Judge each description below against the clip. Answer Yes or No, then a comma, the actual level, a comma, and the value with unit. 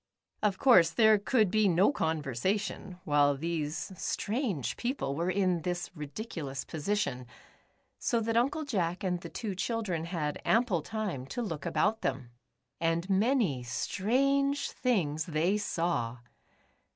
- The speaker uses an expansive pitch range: Yes, wide, 6.0 semitones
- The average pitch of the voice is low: No, medium, 185 Hz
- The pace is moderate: No, slow, 130 wpm